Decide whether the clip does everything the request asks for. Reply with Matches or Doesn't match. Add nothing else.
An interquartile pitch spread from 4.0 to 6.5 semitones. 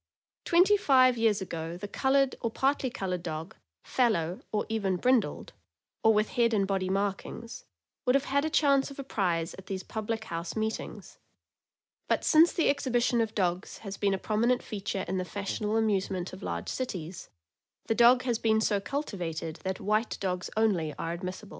Matches